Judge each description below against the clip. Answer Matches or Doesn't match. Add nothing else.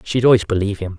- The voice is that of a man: Matches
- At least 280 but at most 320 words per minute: Doesn't match